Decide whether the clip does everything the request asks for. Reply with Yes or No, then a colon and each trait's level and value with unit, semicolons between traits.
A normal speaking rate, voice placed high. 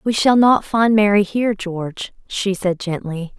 Yes: average, 175 wpm; high, 200 Hz